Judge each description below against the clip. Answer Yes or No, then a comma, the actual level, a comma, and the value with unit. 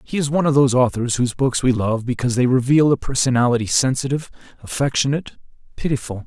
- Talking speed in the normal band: Yes, average, 170 wpm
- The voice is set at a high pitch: No, low, 130 Hz